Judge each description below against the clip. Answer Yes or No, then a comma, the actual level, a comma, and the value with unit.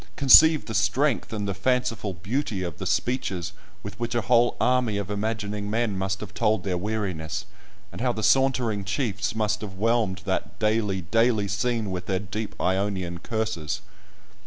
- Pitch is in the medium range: No, low, 105 Hz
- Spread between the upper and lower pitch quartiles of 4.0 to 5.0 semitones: No, average, 3.2 semitones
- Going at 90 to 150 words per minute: No, average, 165 wpm